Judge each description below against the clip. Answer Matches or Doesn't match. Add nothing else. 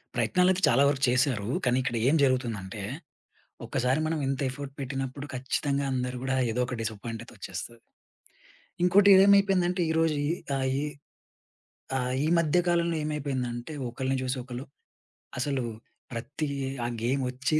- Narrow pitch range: Doesn't match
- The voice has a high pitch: Doesn't match